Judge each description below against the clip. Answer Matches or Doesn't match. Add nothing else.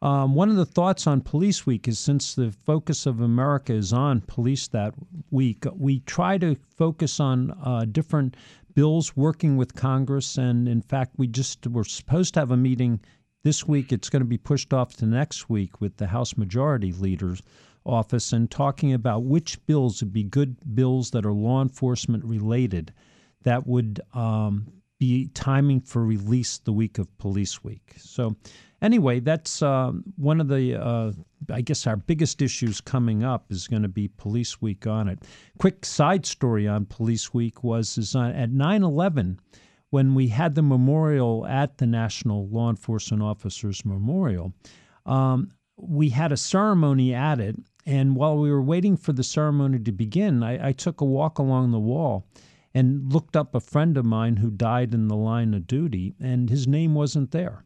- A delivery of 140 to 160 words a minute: Doesn't match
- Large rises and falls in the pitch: Doesn't match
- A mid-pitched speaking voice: Doesn't match